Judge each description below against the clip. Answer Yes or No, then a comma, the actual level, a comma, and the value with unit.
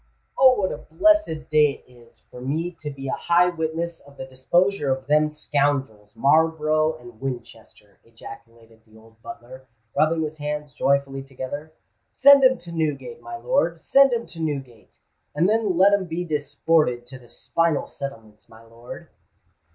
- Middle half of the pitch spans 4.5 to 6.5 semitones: Yes, average, 4.9 semitones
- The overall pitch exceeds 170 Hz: No, medium, 145 Hz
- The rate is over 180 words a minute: No, average, 160 wpm